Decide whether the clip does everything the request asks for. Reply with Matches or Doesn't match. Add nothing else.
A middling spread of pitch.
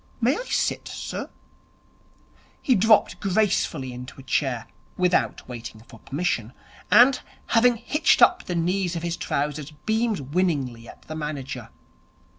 Doesn't match